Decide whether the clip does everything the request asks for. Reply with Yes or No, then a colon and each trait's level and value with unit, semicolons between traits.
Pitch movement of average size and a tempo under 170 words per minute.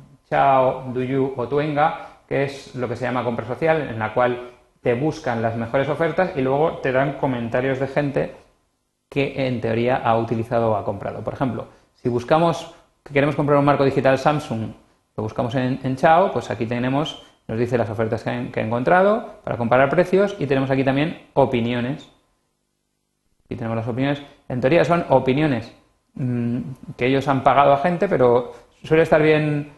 No: average, 3.3 semitones; average, 180 wpm